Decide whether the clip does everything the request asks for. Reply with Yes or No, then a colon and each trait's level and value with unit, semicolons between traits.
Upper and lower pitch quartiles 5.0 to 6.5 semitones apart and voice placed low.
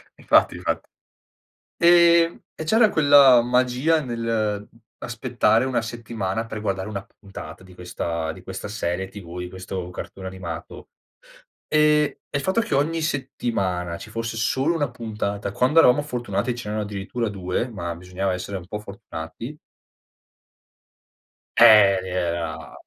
Yes: wide, 5.6 semitones; low, 110 Hz